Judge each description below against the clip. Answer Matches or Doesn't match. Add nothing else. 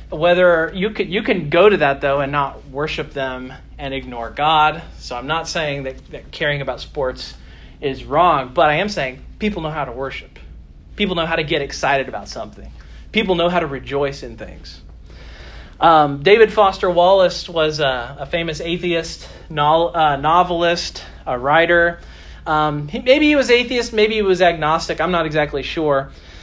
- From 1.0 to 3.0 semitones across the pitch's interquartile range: Doesn't match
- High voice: Doesn't match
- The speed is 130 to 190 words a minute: Matches